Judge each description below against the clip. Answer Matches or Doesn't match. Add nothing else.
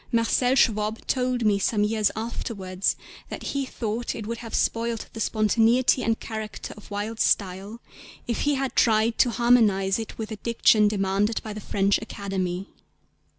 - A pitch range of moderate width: Doesn't match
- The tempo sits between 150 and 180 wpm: Matches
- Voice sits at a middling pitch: Doesn't match